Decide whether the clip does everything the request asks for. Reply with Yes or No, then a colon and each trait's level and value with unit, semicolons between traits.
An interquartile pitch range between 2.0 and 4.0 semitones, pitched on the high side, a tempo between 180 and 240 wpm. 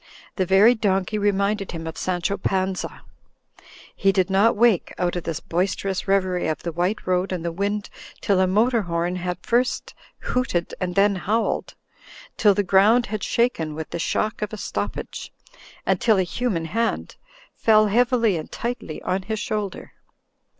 No: average, 3.2 semitones; high, 195 Hz; average, 165 wpm